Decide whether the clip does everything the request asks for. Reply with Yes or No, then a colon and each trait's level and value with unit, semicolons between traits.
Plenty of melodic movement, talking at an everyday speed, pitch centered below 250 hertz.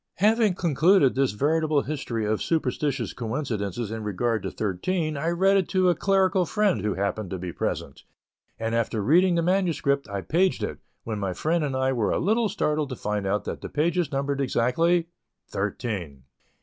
Yes: wide, 8.0 semitones; average, 175 wpm; medium, 140 Hz